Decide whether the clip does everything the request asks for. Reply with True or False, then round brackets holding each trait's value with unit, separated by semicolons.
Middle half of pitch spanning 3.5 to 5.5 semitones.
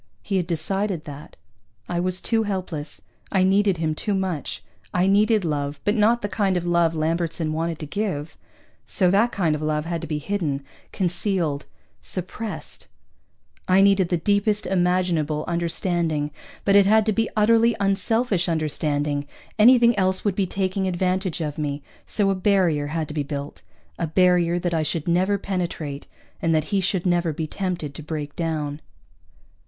True (4.0 semitones)